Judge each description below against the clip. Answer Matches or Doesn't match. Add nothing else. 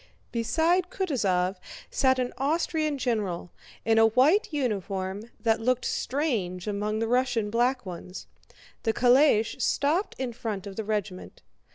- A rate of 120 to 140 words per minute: Matches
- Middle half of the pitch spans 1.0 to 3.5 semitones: Doesn't match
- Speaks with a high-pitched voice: Matches